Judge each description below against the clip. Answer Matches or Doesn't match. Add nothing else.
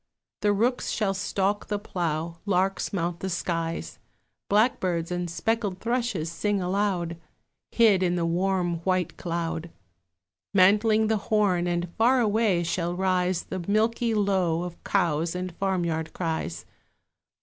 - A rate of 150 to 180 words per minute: Doesn't match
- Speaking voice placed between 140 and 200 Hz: Matches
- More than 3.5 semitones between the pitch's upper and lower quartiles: Doesn't match